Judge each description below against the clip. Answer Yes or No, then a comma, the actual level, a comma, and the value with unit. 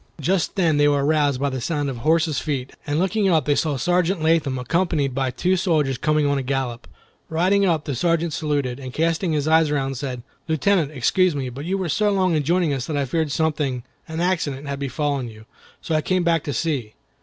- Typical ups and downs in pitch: Yes, average, 3.4 semitones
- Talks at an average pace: No, fast, 215 wpm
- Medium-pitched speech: Yes, medium, 150 Hz